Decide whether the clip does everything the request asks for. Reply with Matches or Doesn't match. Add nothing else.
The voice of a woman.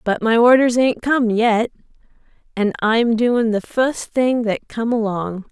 Matches